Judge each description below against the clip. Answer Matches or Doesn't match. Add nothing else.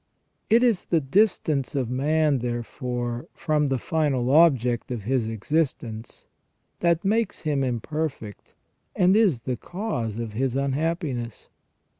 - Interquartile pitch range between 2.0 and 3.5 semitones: Doesn't match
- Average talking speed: Doesn't match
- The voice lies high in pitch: Doesn't match